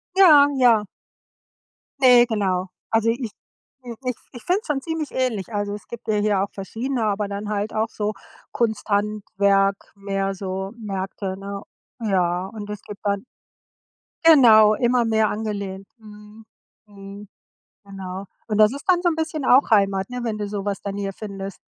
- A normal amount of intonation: Yes, average, 3.0 semitones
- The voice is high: Yes, high, 210 Hz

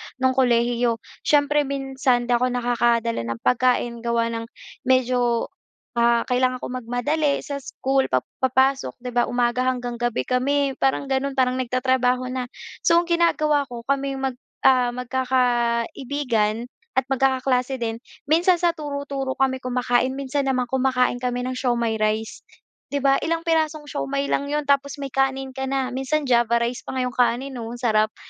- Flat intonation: Yes, narrow, 2.2 semitones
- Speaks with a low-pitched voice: No, very high, 255 Hz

